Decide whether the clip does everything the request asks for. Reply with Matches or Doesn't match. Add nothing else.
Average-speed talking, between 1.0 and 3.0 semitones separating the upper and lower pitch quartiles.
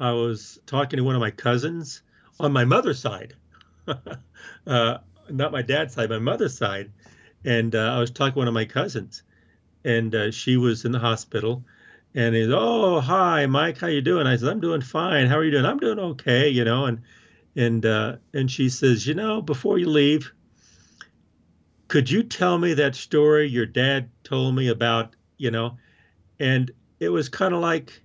Doesn't match